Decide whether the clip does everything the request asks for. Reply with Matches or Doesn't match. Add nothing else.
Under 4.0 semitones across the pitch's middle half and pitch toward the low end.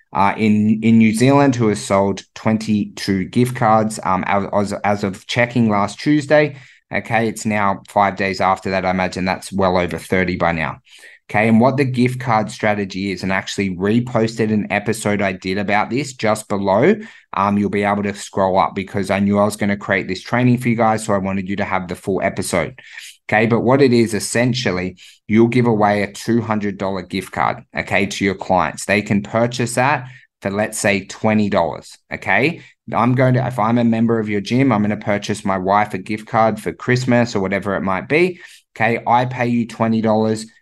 Matches